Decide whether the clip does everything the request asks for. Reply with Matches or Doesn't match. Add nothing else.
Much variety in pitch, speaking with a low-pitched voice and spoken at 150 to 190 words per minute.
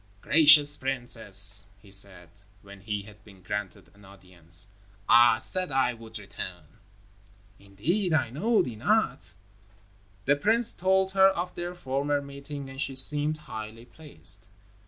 Doesn't match